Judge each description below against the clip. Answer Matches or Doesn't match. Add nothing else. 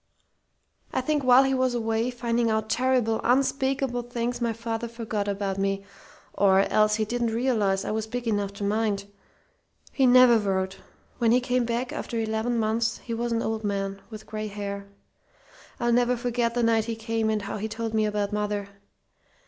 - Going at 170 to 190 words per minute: Matches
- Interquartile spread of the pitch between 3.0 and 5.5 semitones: Doesn't match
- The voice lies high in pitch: Matches